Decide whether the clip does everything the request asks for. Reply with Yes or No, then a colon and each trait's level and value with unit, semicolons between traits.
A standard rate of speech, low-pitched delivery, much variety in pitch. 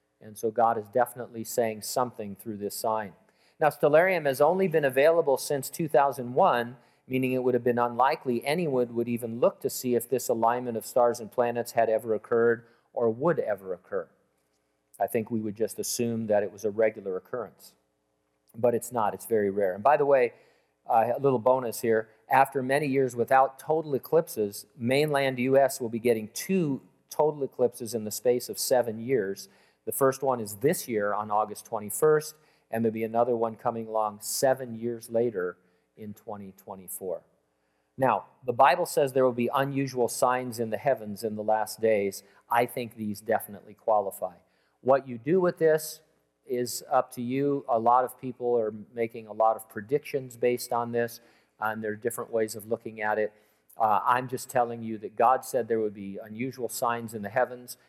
No: average, 185 wpm; low, 120 Hz; average, 3.0 semitones